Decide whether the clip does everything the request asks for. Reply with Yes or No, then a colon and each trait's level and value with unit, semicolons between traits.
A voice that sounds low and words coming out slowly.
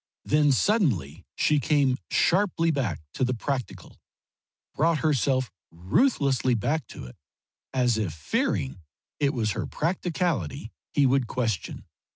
Yes: low, 130 Hz; slow, 125 wpm